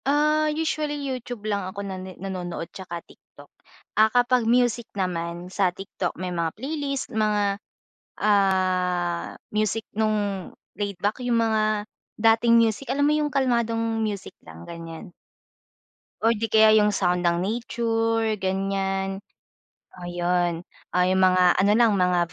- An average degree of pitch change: Yes, average, 3.9 semitones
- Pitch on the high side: Yes, high, 205 Hz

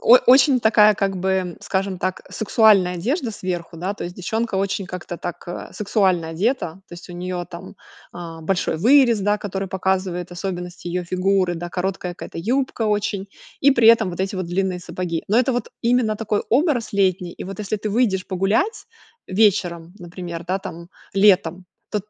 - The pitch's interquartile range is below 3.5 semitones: Yes, average, 3.1 semitones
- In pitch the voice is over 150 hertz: Yes, high, 190 Hz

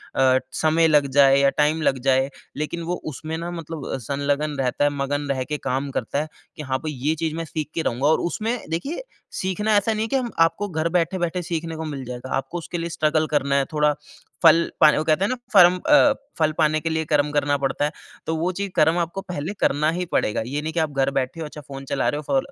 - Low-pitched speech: No, medium, 155 Hz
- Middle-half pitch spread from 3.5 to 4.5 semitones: No, average, 2.9 semitones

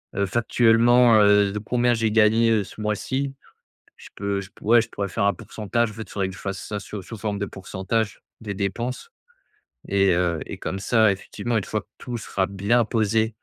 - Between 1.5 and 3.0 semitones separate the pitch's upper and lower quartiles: Yes, narrow, 2.6 semitones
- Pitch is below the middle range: Yes, low, 105 Hz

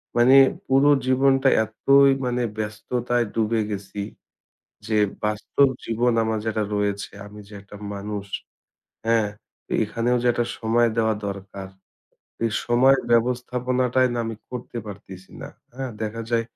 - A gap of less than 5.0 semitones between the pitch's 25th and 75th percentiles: Yes, average, 2.9 semitones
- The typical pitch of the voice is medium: No, low, 115 Hz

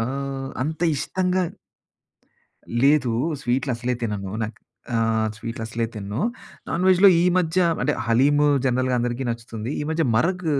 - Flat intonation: No, average, 4.7 semitones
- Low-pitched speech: Yes, low, 130 Hz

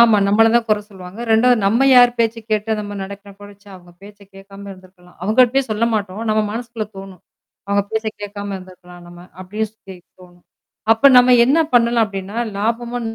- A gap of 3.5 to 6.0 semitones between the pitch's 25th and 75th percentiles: No, average, 2.9 semitones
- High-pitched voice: Yes, high, 210 Hz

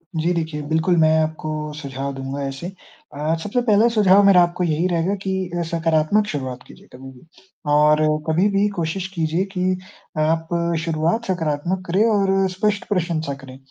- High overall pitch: No, medium, 165 Hz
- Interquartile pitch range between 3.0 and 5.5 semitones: Yes, average, 3.6 semitones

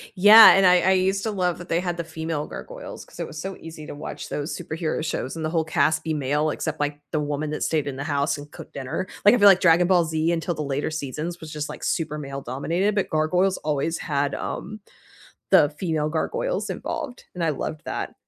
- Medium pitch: Yes, medium, 160 Hz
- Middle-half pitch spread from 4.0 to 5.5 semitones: No, average, 3.2 semitones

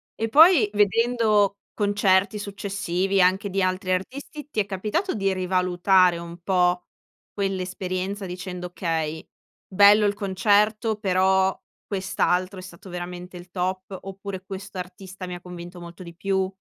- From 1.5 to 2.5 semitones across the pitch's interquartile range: Yes, narrow, 1.9 semitones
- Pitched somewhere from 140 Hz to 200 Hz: Yes, high, 190 Hz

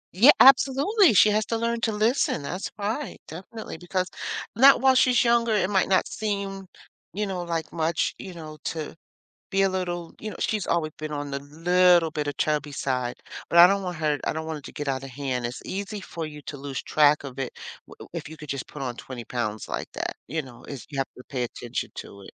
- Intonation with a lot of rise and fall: Yes, wide, 6.0 semitones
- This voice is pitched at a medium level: Yes, medium, 165 Hz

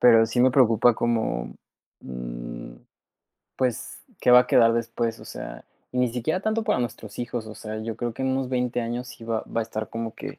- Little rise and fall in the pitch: Yes, narrow, 2.0 semitones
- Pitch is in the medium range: No, low, 115 Hz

